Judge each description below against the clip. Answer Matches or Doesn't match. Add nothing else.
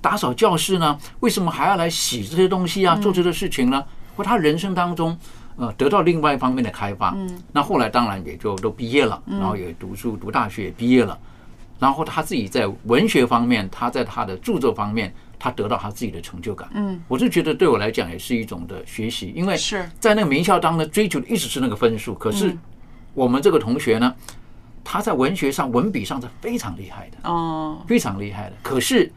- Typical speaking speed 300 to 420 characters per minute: Matches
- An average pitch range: Doesn't match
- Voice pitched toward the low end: Doesn't match